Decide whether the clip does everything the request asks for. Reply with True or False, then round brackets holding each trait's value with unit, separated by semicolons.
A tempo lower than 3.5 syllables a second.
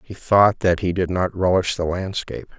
False (5.0 syllables/s)